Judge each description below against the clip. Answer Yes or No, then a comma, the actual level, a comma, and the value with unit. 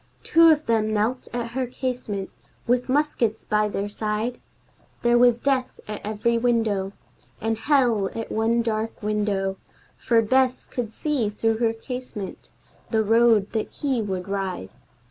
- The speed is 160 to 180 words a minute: No, average, 145 wpm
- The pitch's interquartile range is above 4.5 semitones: No, average, 2.8 semitones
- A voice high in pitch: Yes, high, 225 Hz